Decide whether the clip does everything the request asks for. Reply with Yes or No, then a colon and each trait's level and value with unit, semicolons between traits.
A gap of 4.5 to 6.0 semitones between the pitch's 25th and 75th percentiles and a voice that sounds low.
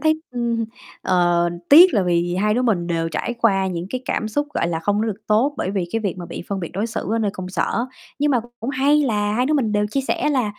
No: average, 5.1 semitones; high, 210 Hz